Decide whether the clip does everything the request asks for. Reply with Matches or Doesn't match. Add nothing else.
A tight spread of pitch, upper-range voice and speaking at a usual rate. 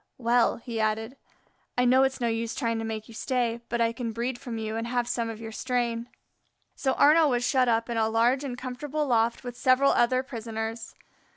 Doesn't match